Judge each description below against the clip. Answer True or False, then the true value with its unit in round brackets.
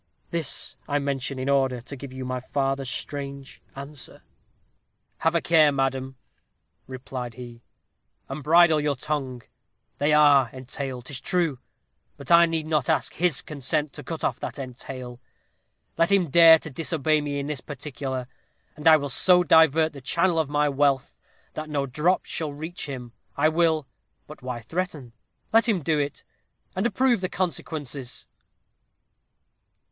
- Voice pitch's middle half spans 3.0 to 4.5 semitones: True (3.3 semitones)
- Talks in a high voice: False (145 Hz)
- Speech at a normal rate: True (155 wpm)